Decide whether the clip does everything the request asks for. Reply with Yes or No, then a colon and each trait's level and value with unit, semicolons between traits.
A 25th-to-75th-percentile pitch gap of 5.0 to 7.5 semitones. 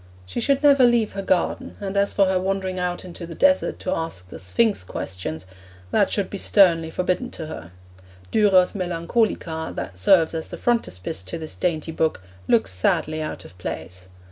No: average, 4.4 semitones